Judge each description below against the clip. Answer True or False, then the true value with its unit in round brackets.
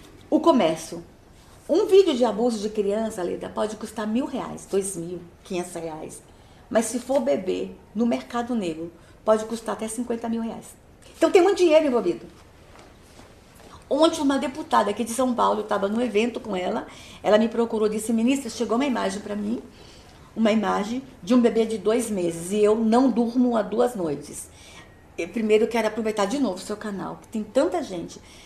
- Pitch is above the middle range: True (225 Hz)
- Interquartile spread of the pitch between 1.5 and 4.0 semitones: True (3.0 semitones)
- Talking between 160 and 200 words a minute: True (185 wpm)